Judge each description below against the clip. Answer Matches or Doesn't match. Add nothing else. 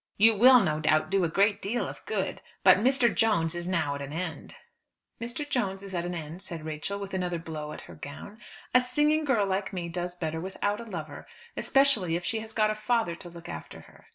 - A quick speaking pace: Matches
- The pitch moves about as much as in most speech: Matches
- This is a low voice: Doesn't match